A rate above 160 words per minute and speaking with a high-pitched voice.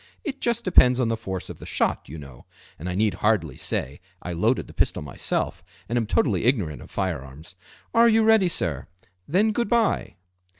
No: average, 200 wpm; low, 110 Hz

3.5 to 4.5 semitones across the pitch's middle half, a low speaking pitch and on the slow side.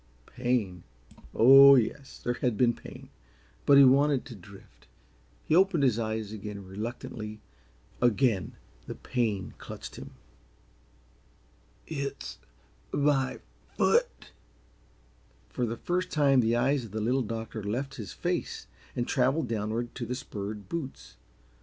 Yes: average, 4.0 semitones; low, 120 Hz; slow, 130 wpm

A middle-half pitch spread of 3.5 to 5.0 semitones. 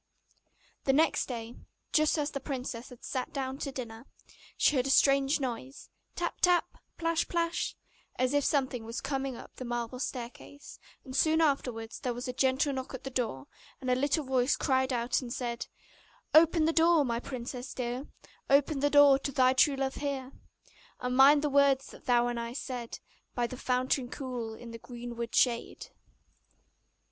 No: narrow, 2.5 semitones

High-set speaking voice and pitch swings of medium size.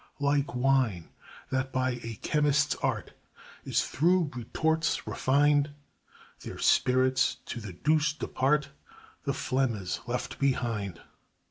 No: low, 135 Hz; average, 3.3 semitones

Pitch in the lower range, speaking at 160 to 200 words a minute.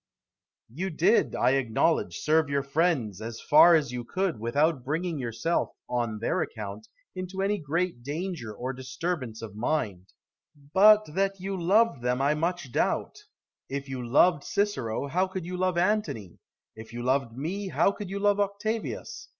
No: medium, 155 Hz; average, 165 wpm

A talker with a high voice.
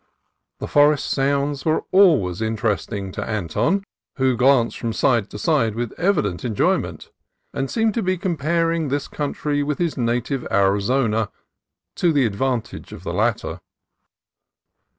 No: low, 135 Hz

